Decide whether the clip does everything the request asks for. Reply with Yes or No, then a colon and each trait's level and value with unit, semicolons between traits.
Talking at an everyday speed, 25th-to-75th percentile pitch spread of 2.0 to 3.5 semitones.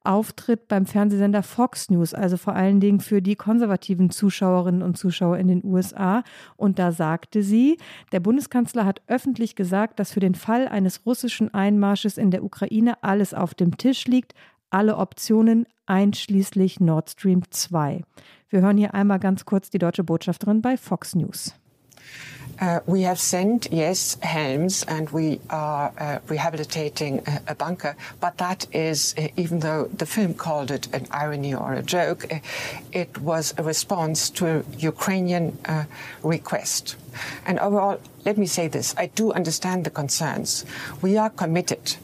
No: average, 160 wpm; average, 4.2 semitones